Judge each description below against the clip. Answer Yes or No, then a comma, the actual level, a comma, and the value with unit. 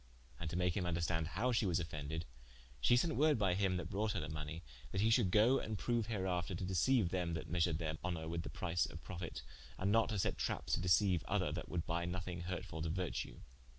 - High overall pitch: No, very low, 90 Hz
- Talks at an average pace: No, fast, 230 wpm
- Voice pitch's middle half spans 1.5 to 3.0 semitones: No, average, 3.6 semitones